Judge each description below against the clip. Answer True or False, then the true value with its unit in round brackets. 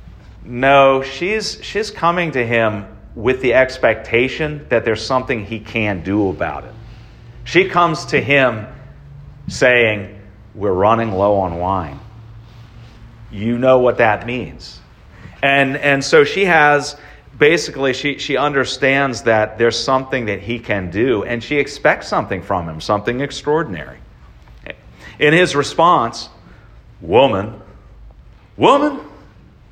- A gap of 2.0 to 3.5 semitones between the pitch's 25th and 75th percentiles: False (4.5 semitones)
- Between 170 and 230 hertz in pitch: False (120 Hz)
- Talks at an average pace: False (125 wpm)